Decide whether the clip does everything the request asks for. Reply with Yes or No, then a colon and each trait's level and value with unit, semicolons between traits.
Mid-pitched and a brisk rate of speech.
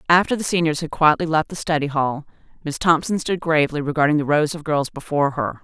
Yes: medium, 155 Hz; fast, 215 wpm